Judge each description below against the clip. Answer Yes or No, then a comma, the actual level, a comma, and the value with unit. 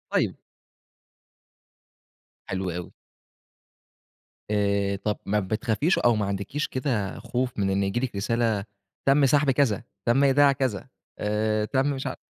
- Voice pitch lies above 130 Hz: No, low, 110 Hz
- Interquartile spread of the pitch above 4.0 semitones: Yes, average, 4.9 semitones